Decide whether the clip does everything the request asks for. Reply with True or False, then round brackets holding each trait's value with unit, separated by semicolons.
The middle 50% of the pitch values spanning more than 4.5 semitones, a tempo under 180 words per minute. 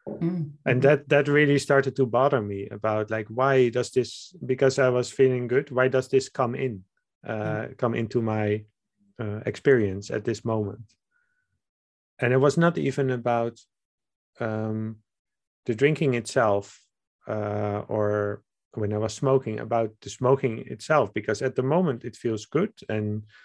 False (3.7 semitones; 155 wpm)